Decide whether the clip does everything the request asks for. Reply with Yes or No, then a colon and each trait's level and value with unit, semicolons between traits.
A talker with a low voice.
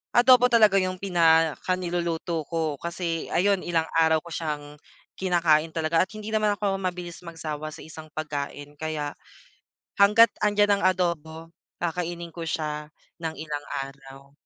No: medium, 165 Hz